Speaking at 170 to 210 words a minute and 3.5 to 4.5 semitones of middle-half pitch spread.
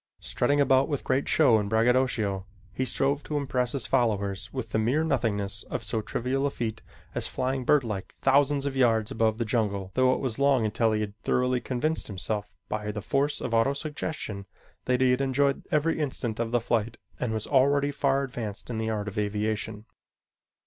Yes: average, 190 wpm; average, 4.0 semitones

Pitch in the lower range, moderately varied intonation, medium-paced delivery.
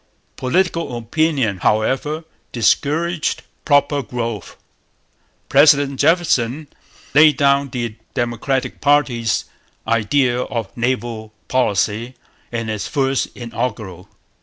No: low, 125 Hz; average, 3.8 semitones; slow, 85 wpm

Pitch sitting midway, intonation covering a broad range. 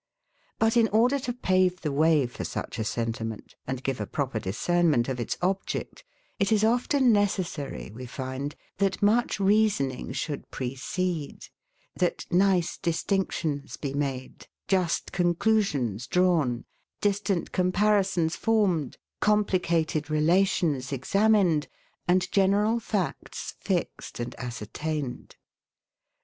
Yes: medium, 175 Hz; wide, 6.6 semitones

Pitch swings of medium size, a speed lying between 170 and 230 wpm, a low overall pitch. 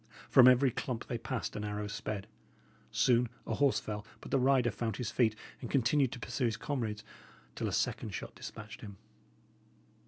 Yes: average, 3.2 semitones; average, 180 wpm; low, 120 Hz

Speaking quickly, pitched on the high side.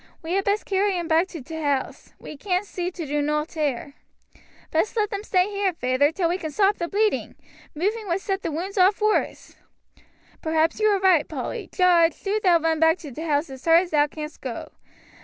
Yes: fast, 215 wpm; very high, 340 Hz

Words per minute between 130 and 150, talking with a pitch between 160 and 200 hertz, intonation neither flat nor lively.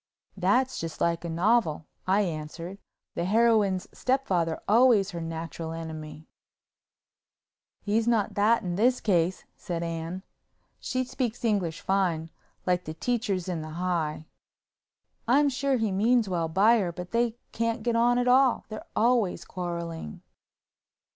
No: slow, 135 wpm; high, 190 Hz; wide, 5.7 semitones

